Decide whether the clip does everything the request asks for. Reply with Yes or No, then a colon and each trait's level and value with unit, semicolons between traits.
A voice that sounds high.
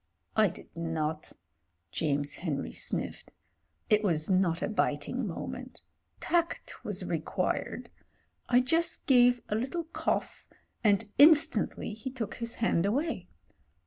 Yes: high, 215 Hz